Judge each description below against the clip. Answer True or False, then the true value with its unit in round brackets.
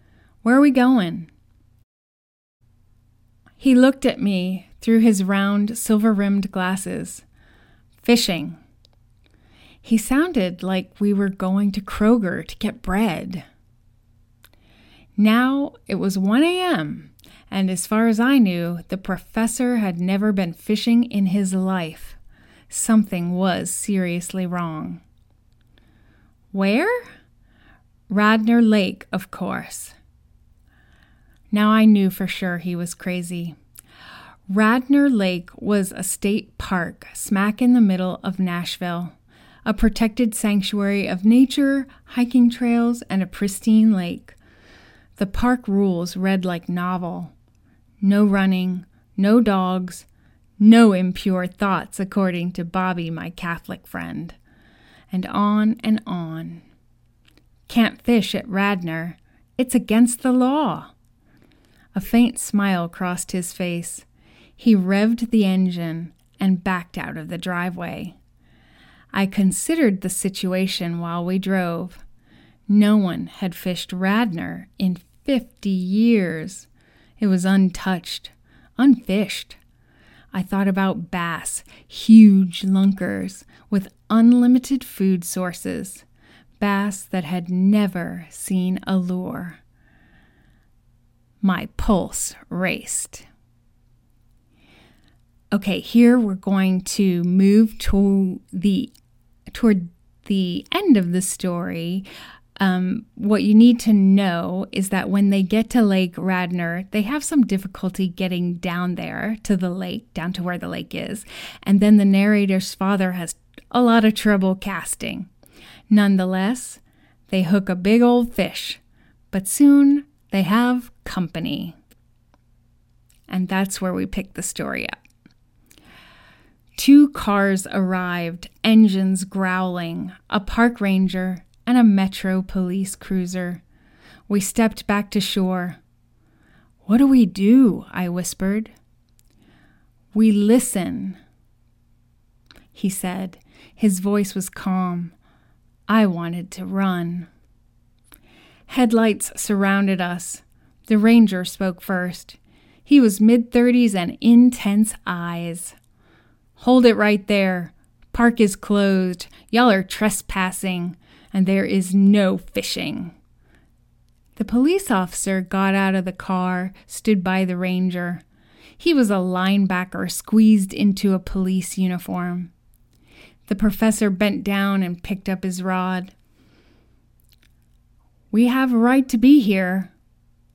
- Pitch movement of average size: True (3.3 semitones)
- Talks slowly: True (115 wpm)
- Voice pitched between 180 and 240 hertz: True (190 Hz)